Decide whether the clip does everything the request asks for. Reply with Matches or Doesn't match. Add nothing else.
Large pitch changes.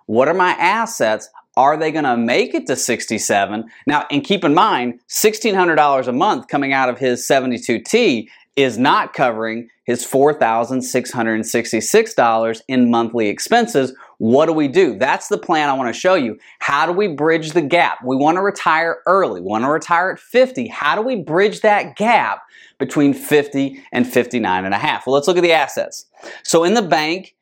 Matches